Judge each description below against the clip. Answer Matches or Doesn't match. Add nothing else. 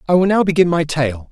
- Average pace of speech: Doesn't match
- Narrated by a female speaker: Doesn't match